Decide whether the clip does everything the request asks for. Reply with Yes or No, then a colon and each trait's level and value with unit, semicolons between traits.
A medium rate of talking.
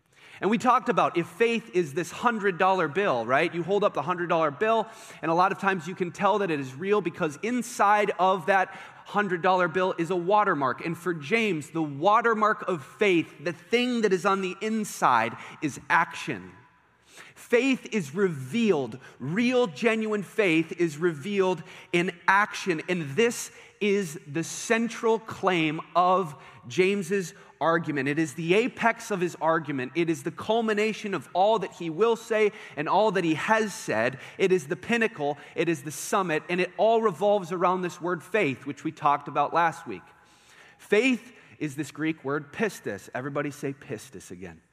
Yes: average, 170 wpm